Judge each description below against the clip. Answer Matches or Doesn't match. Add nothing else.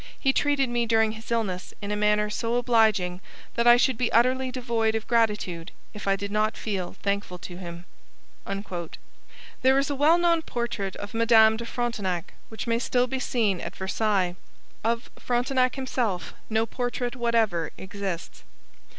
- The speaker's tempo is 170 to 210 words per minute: Doesn't match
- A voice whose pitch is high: Matches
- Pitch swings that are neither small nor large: Matches